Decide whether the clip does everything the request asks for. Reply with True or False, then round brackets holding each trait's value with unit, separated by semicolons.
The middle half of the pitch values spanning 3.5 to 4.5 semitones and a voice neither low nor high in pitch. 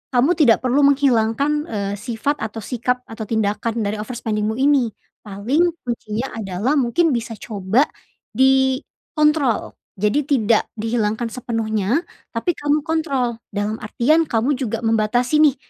False (4.2 semitones; 235 Hz)